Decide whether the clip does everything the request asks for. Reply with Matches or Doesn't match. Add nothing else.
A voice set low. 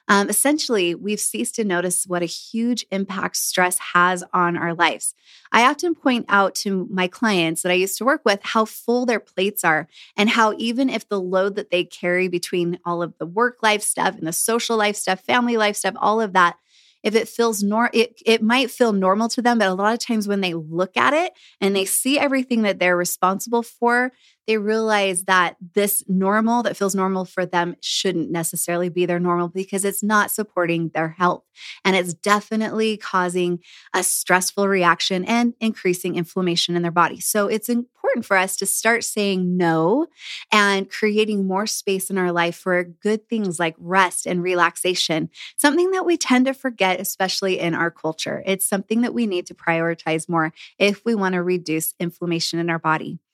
Doesn't match